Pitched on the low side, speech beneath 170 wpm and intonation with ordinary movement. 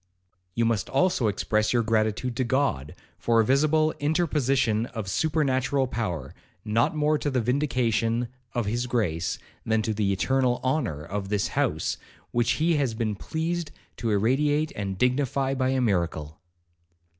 Yes: low, 120 Hz; average, 150 wpm; average, 4.3 semitones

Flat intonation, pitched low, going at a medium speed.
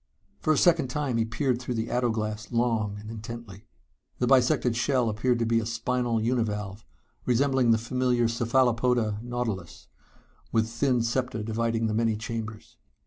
Yes: narrow, 1.9 semitones; low, 115 Hz; average, 155 wpm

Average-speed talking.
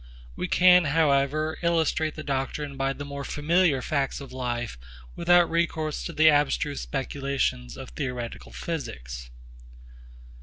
No: slow, 125 wpm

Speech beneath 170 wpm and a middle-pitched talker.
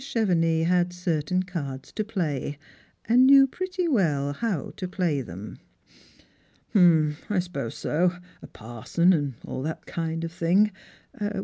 Yes: average, 140 wpm; medium, 170 Hz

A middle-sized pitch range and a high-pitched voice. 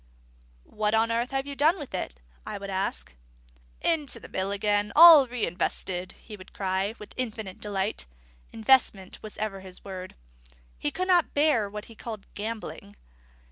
Yes: average, 4.5 semitones; high, 210 Hz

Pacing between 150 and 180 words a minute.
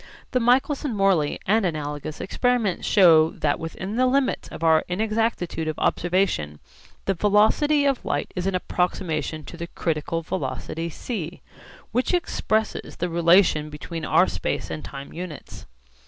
No: average, 140 wpm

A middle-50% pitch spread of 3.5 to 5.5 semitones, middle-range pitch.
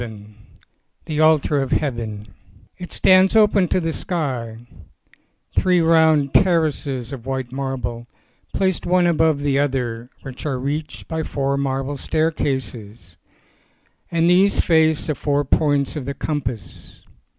Yes: average, 3.9 semitones; medium, 145 Hz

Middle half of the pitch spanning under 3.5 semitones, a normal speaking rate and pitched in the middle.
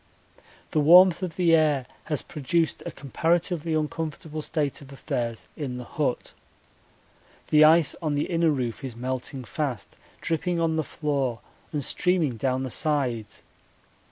No: average, 3.8 semitones; average, 145 wpm; medium, 150 Hz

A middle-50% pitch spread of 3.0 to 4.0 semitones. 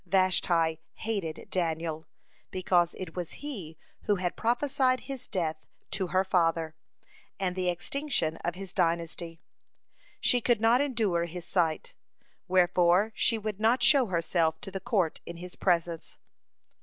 No: average, 4.4 semitones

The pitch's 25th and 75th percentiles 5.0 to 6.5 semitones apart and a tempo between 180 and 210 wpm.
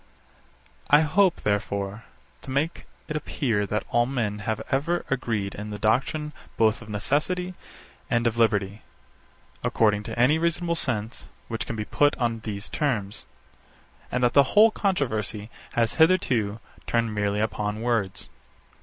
No: wide, 5.6 semitones; average, 145 wpm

